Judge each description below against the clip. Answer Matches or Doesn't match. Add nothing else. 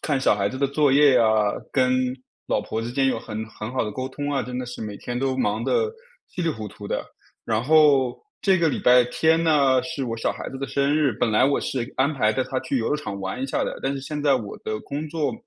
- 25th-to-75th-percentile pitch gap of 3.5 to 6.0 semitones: Matches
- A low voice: Matches